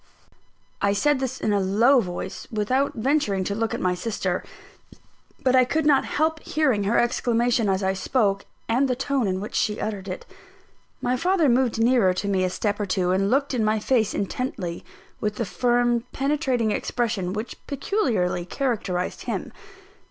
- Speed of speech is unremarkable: Yes, average, 175 wpm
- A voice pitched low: No, high, 225 Hz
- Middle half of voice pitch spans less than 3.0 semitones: No, average, 4.7 semitones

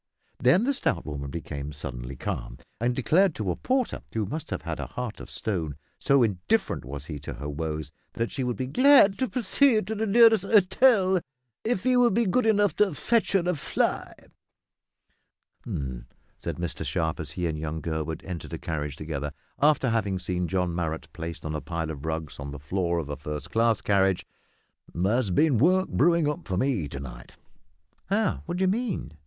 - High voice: No, low, 100 Hz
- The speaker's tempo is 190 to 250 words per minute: Yes, average, 195 wpm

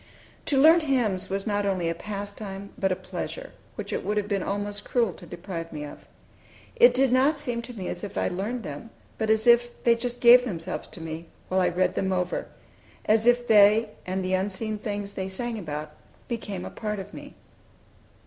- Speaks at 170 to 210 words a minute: Yes, fast, 205 wpm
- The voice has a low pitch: No, high, 205 Hz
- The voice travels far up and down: No, average, 4.1 semitones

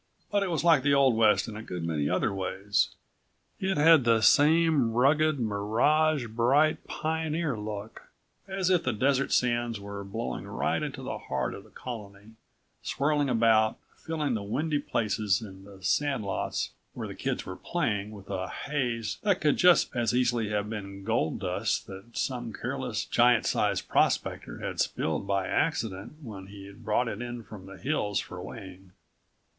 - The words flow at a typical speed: Yes, average, 170 wpm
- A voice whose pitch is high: No, low, 115 Hz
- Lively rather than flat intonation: Yes, wide, 6.1 semitones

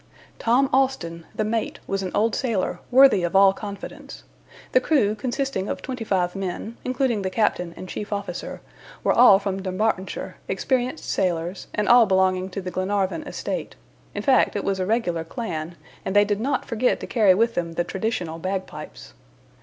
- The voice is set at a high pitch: Yes, high, 200 Hz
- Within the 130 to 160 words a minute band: No, average, 175 wpm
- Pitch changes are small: No, average, 3.9 semitones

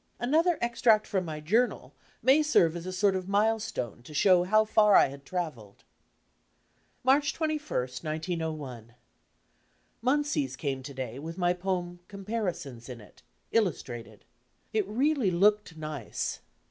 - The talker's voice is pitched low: No, medium, 185 Hz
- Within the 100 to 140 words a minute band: Yes, slow, 135 wpm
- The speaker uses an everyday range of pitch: No, wide, 6.6 semitones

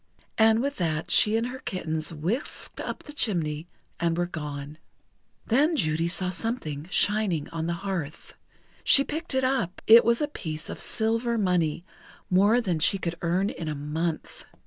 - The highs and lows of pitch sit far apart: Yes, wide, 6.2 semitones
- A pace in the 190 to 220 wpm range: No, average, 170 wpm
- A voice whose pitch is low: No, medium, 180 Hz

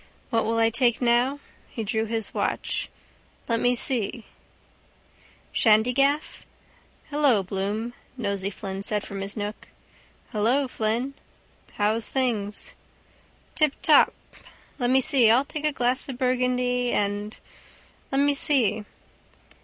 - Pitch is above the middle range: Yes, high, 235 Hz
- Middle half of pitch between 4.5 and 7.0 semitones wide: No, average, 3.5 semitones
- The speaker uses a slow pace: Yes, slow, 120 wpm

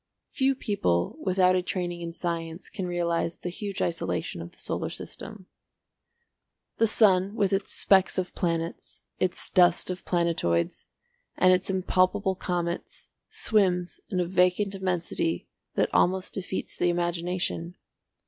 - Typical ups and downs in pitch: No, narrow, 1.9 semitones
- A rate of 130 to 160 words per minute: Yes, slow, 135 wpm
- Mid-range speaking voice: Yes, medium, 180 Hz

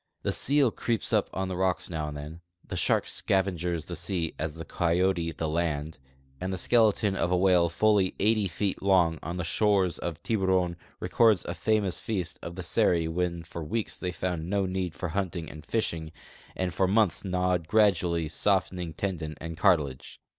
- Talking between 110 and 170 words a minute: No, average, 180 wpm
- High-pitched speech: No, very low, 90 Hz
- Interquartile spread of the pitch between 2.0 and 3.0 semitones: Yes, narrow, 2.6 semitones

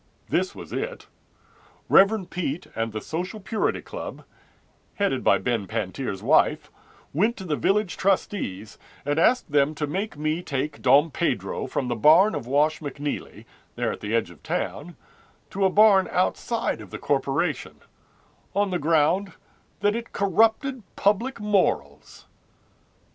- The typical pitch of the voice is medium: Yes, medium, 175 Hz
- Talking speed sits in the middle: Yes, average, 145 wpm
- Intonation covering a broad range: Yes, wide, 6.3 semitones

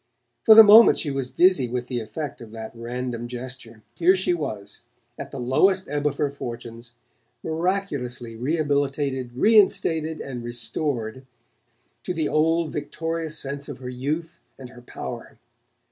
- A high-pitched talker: No, medium, 140 Hz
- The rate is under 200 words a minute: Yes, average, 145 wpm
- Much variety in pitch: No, average, 4.9 semitones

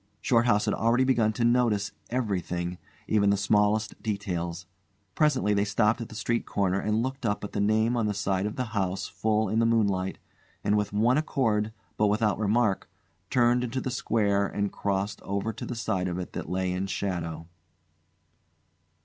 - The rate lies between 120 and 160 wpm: No, average, 180 wpm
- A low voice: Yes, low, 105 Hz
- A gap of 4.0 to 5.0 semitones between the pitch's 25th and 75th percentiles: No, average, 2.7 semitones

